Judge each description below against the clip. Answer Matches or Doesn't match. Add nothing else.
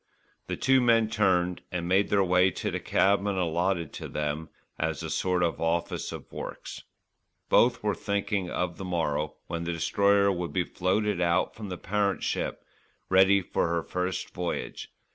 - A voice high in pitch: Doesn't match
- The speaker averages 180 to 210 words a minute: Doesn't match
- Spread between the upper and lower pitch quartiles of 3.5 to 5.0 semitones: Doesn't match